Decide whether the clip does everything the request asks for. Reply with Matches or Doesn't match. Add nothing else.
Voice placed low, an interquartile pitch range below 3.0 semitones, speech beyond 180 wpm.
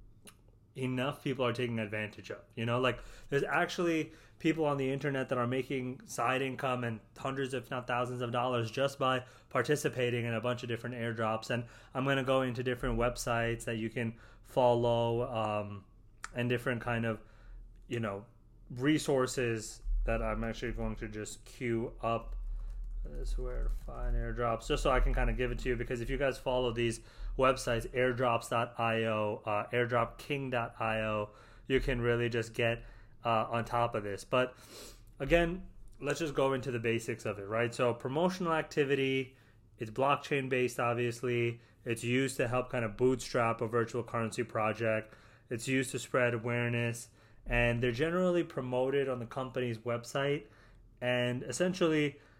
Doesn't match